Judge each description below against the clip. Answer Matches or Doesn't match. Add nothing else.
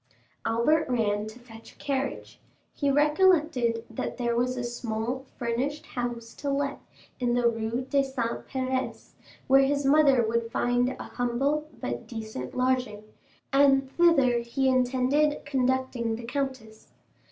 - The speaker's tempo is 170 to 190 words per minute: Doesn't match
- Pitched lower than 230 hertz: Doesn't match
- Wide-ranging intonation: Doesn't match